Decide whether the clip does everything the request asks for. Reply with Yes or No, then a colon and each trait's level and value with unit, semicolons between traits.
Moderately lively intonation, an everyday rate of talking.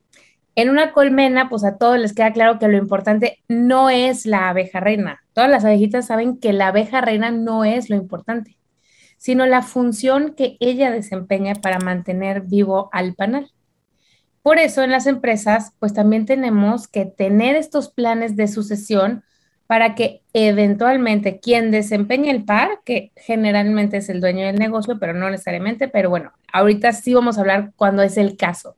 Yes: average, 3.6 semitones; average, 170 wpm